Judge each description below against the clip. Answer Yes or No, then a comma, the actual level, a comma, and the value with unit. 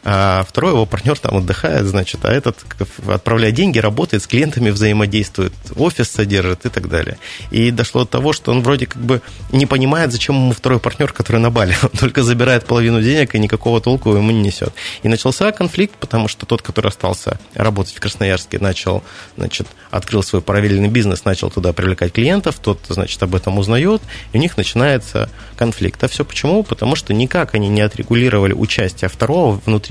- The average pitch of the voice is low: Yes, low, 110 Hz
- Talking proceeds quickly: Yes, fast, 185 wpm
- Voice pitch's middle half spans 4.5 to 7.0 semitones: No, average, 3.7 semitones